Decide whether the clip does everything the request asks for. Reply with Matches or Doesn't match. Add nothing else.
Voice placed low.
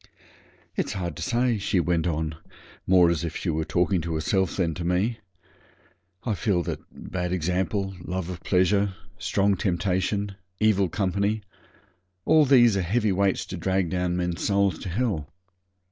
Matches